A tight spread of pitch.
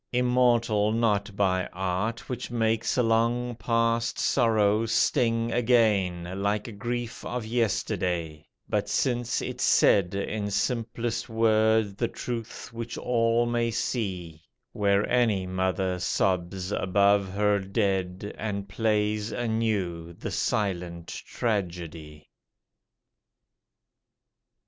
No: average, 3.4 semitones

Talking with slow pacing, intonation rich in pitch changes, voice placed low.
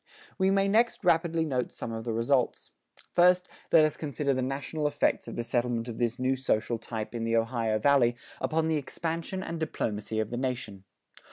No: average, 190 wpm; wide, 5.7 semitones; low, 130 Hz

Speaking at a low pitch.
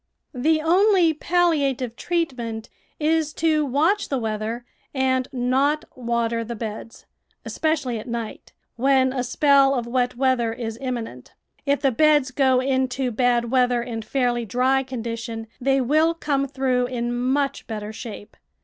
No: very high, 255 Hz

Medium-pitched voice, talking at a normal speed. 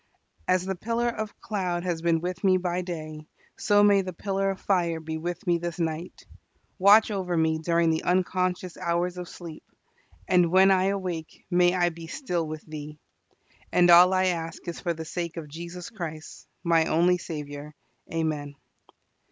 Yes: medium, 175 Hz; average, 175 wpm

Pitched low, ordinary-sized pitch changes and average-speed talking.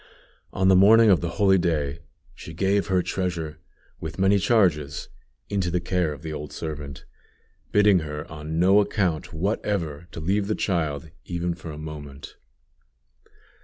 Yes: very low, 85 Hz; average, 3.9 semitones; average, 155 wpm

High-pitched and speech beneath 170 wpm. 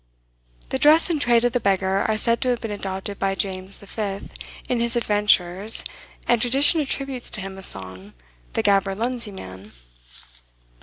Yes: high, 210 Hz; average, 160 wpm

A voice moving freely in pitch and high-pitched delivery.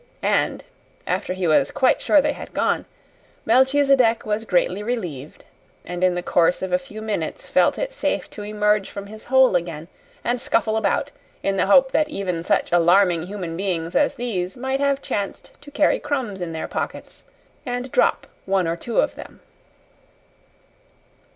Yes: wide, 5.8 semitones; high, 205 Hz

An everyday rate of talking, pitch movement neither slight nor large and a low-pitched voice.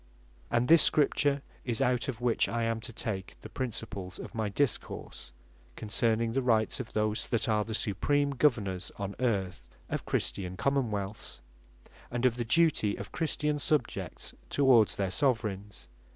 Yes: average, 160 wpm; average, 4.1 semitones; low, 115 Hz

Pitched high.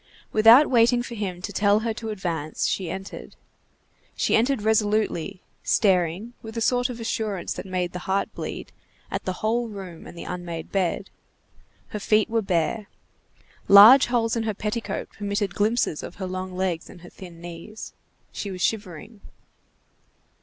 Yes: high, 205 Hz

